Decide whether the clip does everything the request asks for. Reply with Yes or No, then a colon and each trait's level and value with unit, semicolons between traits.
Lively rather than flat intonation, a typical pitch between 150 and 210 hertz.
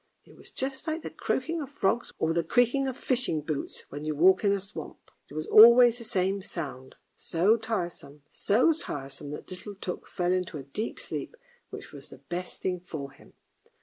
Yes: wide, 7.2 semitones; medium, 185 Hz